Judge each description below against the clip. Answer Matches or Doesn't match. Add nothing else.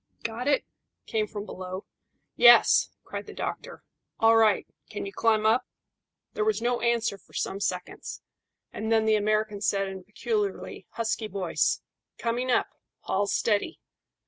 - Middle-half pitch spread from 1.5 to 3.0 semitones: Matches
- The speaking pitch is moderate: Doesn't match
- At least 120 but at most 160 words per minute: Matches